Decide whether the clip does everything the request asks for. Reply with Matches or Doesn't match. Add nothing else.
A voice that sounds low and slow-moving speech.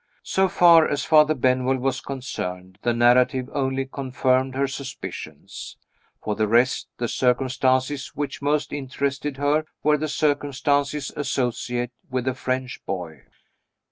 Matches